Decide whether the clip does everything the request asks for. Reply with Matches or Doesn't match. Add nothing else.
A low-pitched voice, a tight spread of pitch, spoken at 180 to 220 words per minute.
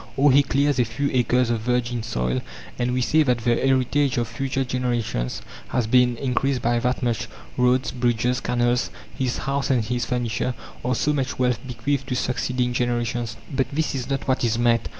Matches